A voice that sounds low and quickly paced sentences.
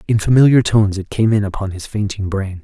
Yes: low, 105 Hz; fast, 230 wpm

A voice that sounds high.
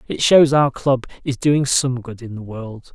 No: low, 125 Hz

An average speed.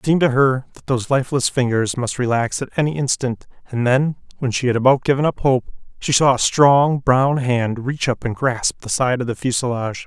No: fast, 220 wpm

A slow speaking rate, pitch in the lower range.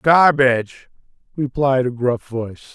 Yes: slow, 110 wpm; low, 130 Hz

